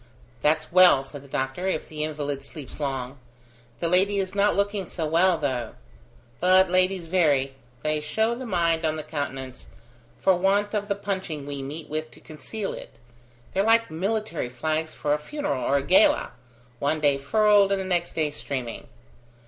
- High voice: No, medium, 160 Hz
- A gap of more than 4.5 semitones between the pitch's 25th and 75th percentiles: Yes, average, 5.1 semitones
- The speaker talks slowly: No, average, 175 wpm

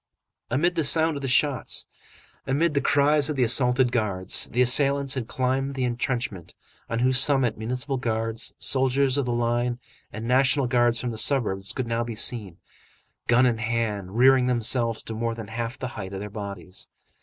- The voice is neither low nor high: No, low, 125 Hz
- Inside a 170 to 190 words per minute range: Yes, average, 180 wpm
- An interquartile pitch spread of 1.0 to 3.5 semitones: Yes, average, 2.7 semitones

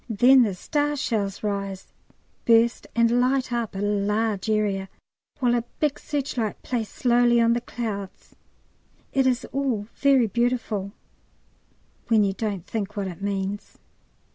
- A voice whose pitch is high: Yes, high, 225 Hz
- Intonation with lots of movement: No, average, 3.3 semitones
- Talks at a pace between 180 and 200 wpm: No, average, 140 wpm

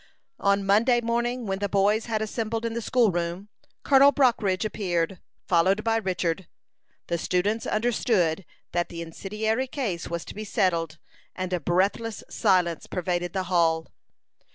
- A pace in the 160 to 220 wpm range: No, average, 150 wpm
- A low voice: No, high, 195 Hz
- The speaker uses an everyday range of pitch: Yes, average, 4.4 semitones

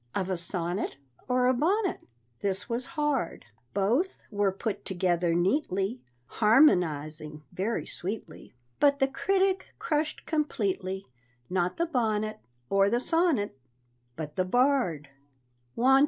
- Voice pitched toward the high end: Yes, high, 210 Hz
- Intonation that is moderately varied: No, wide, 7.4 semitones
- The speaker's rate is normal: No, slow, 115 wpm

